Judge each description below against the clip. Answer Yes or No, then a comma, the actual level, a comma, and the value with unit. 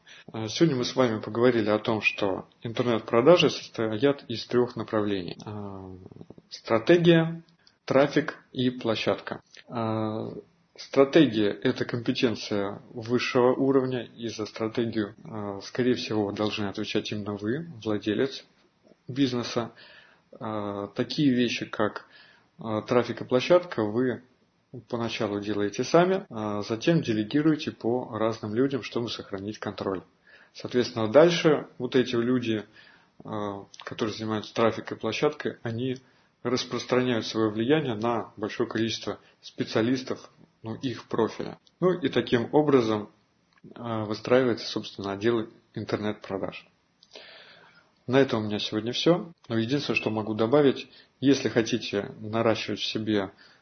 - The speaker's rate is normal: No, slow, 105 wpm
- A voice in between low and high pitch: No, low, 115 Hz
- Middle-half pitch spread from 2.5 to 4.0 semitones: Yes, average, 3.1 semitones